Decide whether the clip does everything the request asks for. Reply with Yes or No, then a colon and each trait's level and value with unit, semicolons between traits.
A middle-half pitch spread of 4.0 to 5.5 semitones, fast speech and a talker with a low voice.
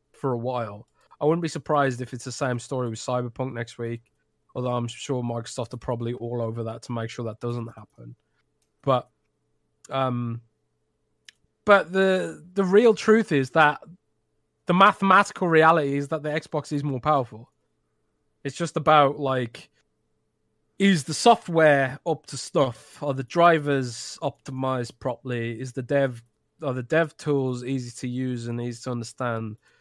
No: average, 4.3 semitones; average, 160 wpm; low, 130 Hz